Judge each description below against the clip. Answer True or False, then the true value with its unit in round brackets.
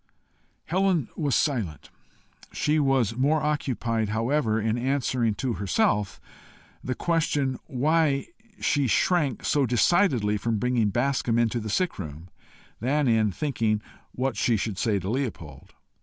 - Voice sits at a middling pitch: False (125 Hz)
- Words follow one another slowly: True (130 wpm)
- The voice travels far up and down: False (4.8 semitones)